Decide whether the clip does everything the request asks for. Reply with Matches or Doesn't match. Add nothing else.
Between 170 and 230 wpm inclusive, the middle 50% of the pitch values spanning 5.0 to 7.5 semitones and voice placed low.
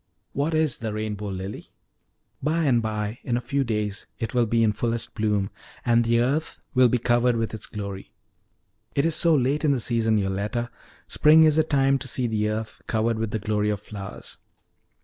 Doesn't match